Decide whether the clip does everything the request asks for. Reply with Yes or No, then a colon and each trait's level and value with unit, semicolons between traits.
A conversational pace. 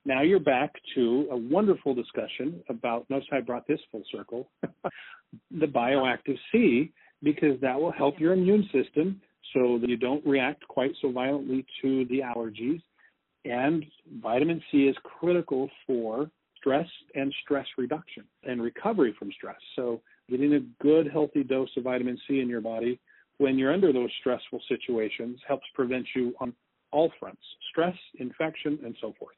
Yes: average, 160 wpm